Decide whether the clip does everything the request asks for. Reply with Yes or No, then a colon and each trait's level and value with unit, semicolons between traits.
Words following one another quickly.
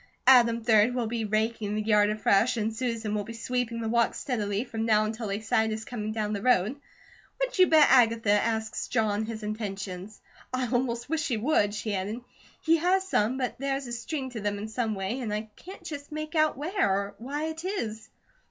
Yes: fast, 210 wpm